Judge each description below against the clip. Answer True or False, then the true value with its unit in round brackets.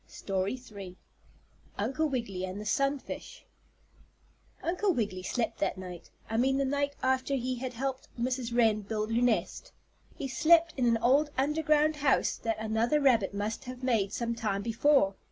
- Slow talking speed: False (165 wpm)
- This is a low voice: False (245 Hz)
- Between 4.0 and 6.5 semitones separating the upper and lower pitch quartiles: True (4.3 semitones)